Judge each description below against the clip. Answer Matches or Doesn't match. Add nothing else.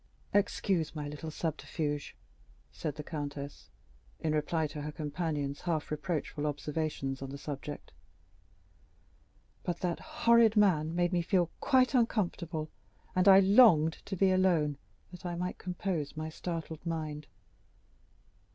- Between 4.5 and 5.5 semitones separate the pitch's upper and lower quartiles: Doesn't match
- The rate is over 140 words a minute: Doesn't match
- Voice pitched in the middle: Matches